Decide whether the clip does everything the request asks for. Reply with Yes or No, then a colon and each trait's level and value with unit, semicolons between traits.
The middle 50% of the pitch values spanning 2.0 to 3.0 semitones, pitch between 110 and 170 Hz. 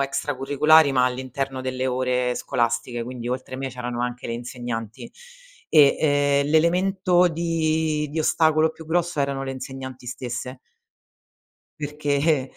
No: average, 3.7 semitones; low, 135 Hz